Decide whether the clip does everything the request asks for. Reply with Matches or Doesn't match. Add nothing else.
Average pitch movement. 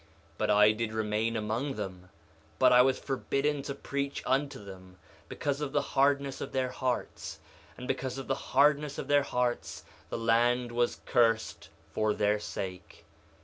Matches